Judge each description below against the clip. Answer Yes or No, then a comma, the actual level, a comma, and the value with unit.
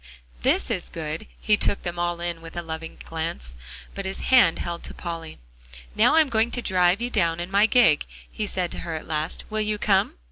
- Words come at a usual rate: No, fast, 215 wpm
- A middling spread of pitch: Yes, average, 4.3 semitones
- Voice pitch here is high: No, medium, 175 Hz